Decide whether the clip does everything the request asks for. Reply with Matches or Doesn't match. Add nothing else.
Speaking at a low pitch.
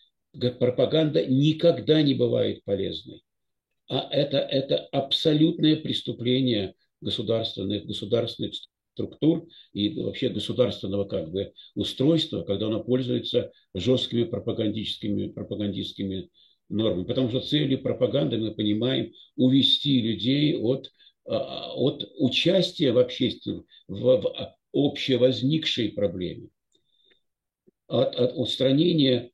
Matches